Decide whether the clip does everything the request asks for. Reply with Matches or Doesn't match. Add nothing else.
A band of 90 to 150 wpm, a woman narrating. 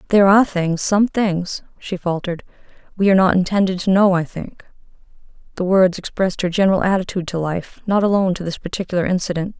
Doesn't match